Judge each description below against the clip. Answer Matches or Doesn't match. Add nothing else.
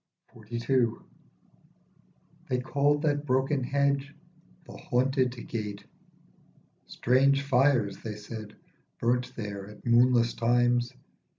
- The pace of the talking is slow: Matches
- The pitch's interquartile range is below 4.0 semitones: Matches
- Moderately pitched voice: Doesn't match